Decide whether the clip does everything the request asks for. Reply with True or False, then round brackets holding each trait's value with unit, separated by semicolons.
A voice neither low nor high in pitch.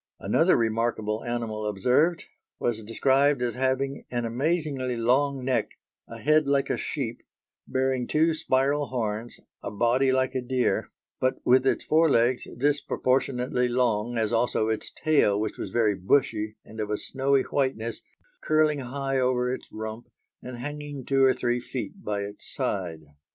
False (125 Hz)